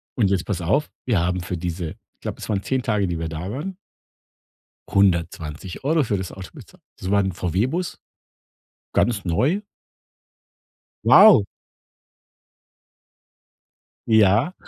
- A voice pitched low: Yes, low, 100 Hz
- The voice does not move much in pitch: No, wide, 5.5 semitones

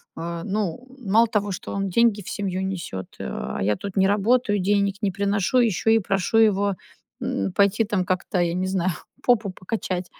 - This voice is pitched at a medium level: No, high, 195 Hz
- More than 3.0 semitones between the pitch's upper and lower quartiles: No, narrow, 2.5 semitones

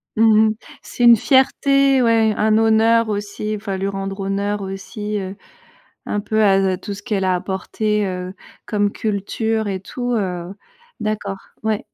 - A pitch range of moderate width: No, narrow, 2.2 semitones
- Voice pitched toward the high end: Yes, high, 210 Hz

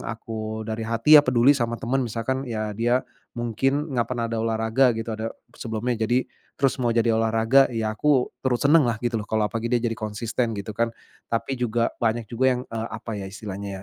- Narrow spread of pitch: Yes, narrow, 2.0 semitones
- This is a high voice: No, low, 115 Hz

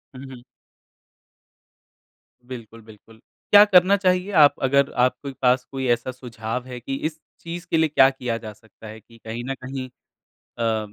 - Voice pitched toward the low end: Yes, low, 130 Hz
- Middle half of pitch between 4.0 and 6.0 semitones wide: No, average, 3.5 semitones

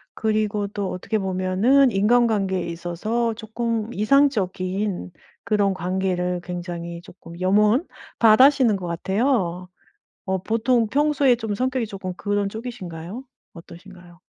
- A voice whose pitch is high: Yes, high, 205 Hz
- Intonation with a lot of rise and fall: No, average, 4.1 semitones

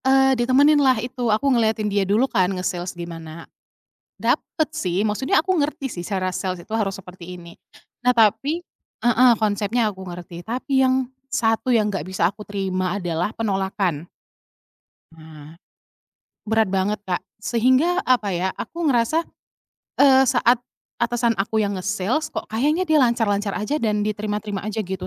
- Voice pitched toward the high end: Yes, high, 215 Hz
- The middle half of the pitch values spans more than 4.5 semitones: Yes, average, 5.0 semitones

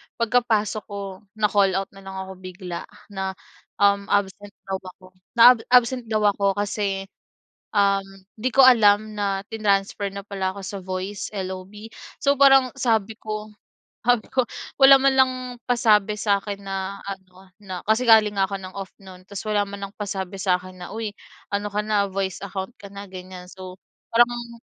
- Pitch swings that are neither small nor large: No, narrow, 2.1 semitones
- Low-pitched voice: No, high, 200 Hz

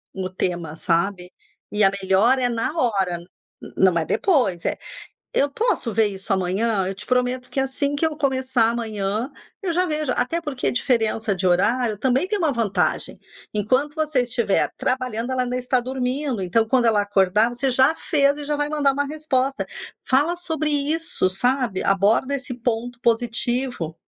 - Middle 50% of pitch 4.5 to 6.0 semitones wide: Yes, average, 5.2 semitones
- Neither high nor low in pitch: No, high, 245 Hz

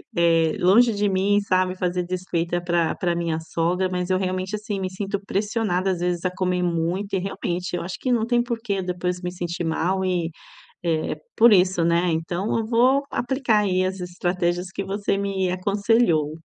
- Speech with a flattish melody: Yes, narrow, 2.3 semitones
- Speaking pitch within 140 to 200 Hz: Yes, medium, 185 Hz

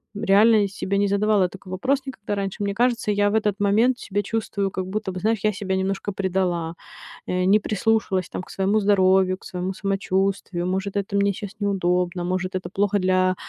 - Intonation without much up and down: Yes, narrow, 1.7 semitones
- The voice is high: Yes, high, 195 Hz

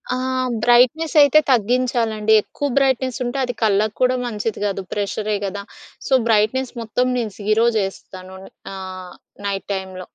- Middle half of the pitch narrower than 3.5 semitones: No, average, 4.0 semitones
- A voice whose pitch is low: No, high, 220 Hz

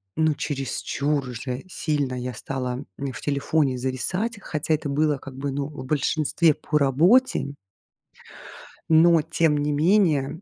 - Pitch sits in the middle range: Yes, medium, 145 Hz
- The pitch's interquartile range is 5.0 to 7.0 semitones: No, average, 2.8 semitones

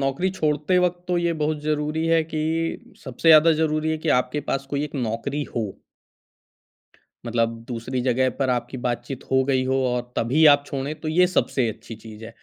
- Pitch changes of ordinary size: Yes, average, 4.0 semitones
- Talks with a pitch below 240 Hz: Yes, medium, 140 Hz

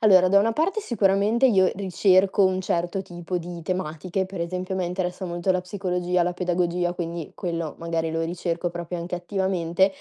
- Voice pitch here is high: No, medium, 180 Hz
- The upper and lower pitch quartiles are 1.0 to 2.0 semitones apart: Yes, narrow, 1.7 semitones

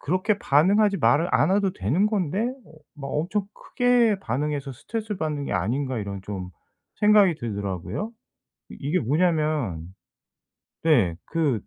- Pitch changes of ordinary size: No, wide, 9.0 semitones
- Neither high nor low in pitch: Yes, medium, 155 Hz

